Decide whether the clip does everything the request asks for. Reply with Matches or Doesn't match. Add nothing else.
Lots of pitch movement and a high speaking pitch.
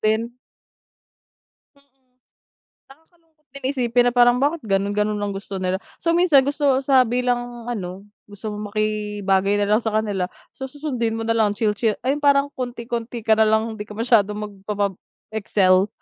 Doesn't match